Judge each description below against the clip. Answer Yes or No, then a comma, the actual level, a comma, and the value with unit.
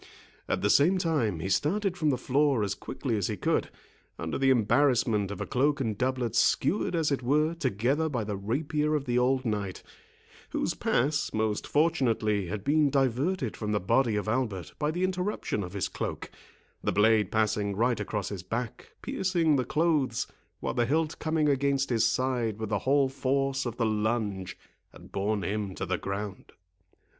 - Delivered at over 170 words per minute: Yes, average, 180 wpm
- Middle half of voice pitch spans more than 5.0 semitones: Yes, wide, 5.5 semitones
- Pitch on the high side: No, low, 125 Hz